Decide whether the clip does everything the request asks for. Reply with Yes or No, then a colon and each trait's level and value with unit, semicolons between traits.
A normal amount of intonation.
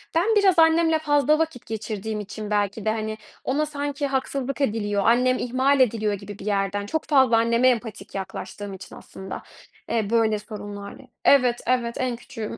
Yes: average, 4.9 semitones